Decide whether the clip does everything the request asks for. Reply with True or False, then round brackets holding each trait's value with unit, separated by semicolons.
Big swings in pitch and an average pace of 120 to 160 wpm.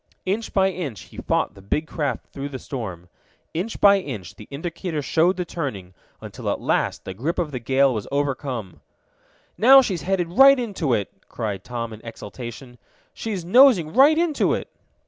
False (8.4 semitones; 175 wpm)